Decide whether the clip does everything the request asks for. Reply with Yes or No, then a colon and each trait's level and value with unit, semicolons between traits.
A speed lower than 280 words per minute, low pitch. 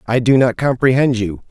Yes: average, 200 wpm; low, 125 Hz